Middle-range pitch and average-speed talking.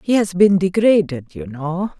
Yes: medium, 175 Hz; average, 180 wpm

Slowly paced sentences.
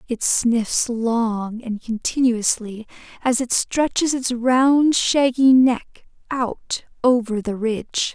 Yes: slow, 120 wpm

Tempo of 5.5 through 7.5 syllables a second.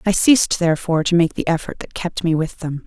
Yes: 6.3 syllables/s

